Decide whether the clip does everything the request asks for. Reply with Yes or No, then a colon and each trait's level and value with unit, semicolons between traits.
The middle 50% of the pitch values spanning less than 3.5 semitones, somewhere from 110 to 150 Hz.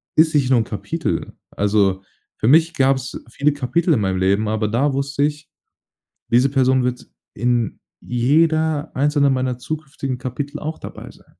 No: average, 3.8 semitones; low, 135 Hz